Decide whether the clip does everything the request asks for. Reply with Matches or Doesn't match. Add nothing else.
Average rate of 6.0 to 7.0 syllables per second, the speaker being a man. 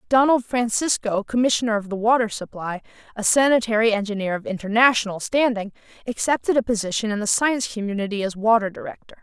Doesn't match